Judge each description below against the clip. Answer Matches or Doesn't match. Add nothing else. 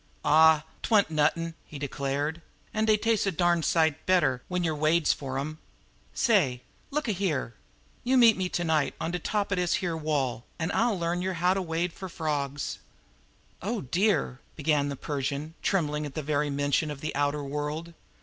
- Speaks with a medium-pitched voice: Matches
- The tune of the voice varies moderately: Matches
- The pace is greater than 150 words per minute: Matches